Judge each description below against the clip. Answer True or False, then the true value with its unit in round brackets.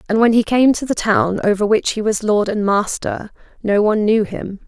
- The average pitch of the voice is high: True (210 Hz)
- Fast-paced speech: True (230 wpm)